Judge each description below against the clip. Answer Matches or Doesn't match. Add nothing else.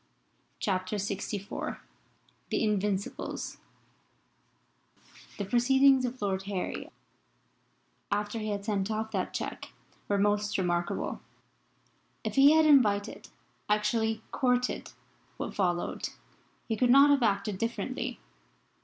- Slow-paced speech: Matches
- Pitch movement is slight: Doesn't match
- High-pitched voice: Matches